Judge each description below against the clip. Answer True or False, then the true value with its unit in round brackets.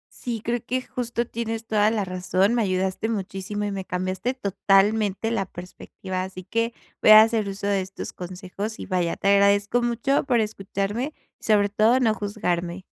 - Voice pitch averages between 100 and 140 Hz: False (205 Hz)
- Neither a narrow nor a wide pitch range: True (3.2 semitones)